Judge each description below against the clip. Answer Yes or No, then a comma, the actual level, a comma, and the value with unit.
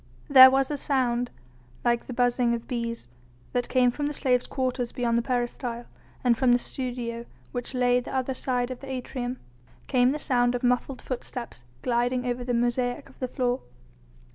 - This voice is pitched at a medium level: No, high, 245 Hz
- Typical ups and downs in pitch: No, narrow, 1.2 semitones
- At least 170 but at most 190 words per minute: Yes, average, 180 wpm